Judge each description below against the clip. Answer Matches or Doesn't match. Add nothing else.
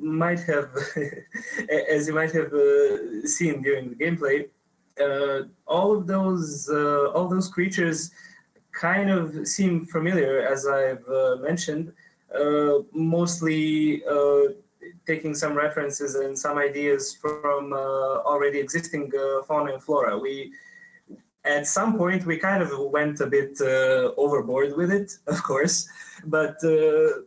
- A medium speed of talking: Matches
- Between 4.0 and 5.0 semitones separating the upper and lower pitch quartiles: Matches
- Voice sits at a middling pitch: Matches